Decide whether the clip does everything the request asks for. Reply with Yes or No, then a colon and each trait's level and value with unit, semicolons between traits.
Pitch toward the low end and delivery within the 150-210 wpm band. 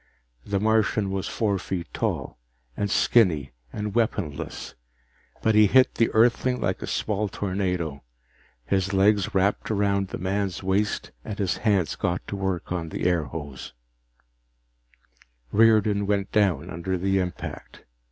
No: low, 100 Hz; slow, 135 wpm